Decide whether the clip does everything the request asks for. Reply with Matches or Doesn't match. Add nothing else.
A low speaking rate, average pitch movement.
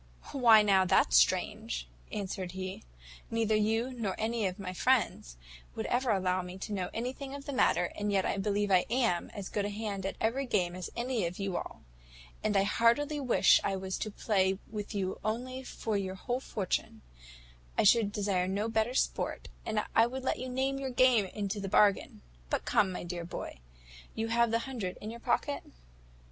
Doesn't match